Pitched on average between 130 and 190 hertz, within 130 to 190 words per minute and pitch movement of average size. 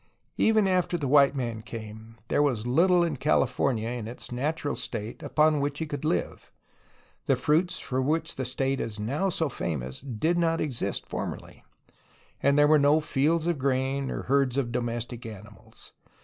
Yes: low, 135 Hz; average, 175 wpm; average, 4.5 semitones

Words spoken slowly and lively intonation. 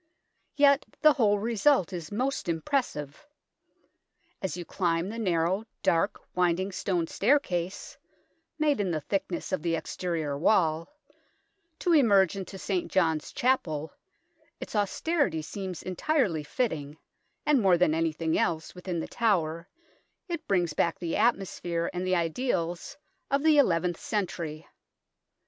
Yes: slow, 130 wpm; wide, 5.7 semitones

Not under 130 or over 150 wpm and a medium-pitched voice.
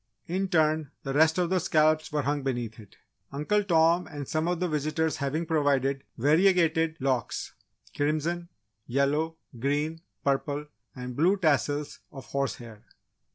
Yes: average, 140 wpm; medium, 150 Hz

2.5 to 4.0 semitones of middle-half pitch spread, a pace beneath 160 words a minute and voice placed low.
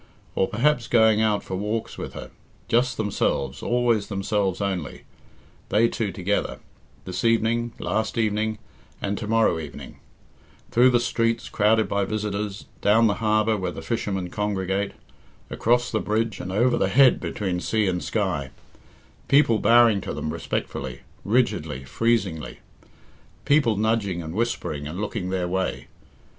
Yes: average, 3.3 semitones; average, 145 wpm; low, 105 Hz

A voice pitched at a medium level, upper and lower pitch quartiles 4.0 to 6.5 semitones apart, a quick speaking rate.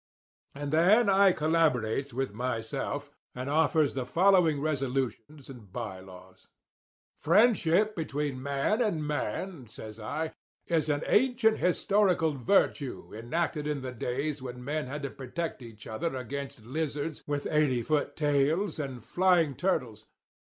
No: medium, 145 Hz; average, 4.5 semitones; slow, 135 wpm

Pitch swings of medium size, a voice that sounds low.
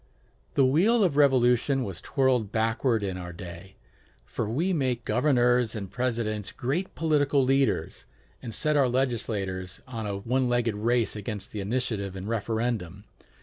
Yes: average, 4.3 semitones; low, 120 Hz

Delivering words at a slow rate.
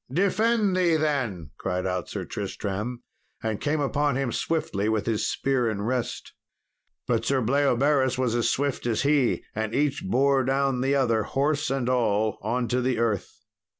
No: average, 165 wpm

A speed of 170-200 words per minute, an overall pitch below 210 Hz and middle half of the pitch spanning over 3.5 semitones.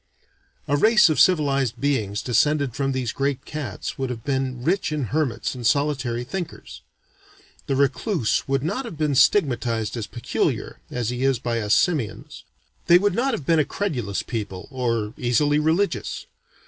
No: average, 160 wpm; low, 135 Hz; average, 4.2 semitones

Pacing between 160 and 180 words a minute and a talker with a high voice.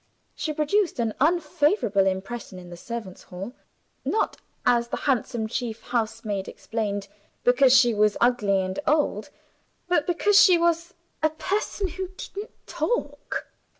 No: slow, 135 wpm; high, 245 Hz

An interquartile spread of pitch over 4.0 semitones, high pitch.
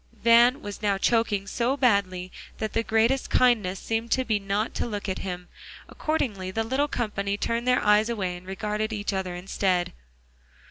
No: average, 3.2 semitones; high, 210 Hz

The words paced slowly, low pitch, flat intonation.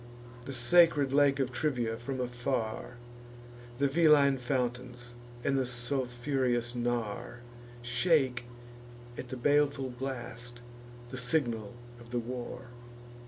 Yes: slow, 105 wpm; low, 125 Hz; narrow, 2.2 semitones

